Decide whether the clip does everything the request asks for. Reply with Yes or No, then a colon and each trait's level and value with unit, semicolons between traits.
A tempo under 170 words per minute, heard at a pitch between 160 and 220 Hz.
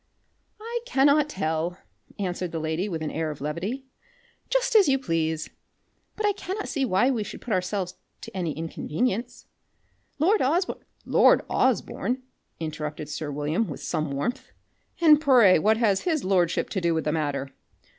Yes: average, 160 wpm; high, 190 Hz